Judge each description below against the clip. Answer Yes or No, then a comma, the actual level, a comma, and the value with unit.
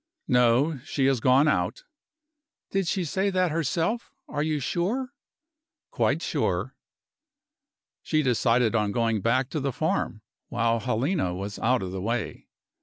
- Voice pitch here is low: Yes, low, 130 Hz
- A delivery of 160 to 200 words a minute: No, average, 140 wpm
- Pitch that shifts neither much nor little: No, wide, 6.0 semitones